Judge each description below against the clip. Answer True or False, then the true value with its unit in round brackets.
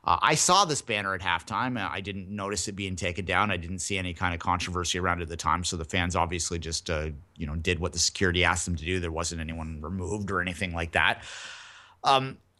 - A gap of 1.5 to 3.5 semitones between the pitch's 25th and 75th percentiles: True (2.7 semitones)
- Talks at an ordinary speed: False (245 wpm)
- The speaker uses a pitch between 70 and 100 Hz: True (90 Hz)